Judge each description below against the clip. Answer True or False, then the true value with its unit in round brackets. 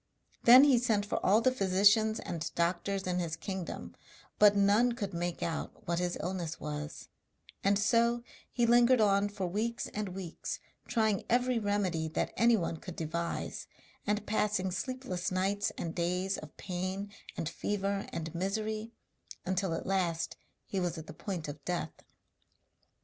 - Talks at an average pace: True (155 wpm)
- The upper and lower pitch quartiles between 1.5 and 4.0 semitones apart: True (3.6 semitones)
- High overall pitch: True (195 Hz)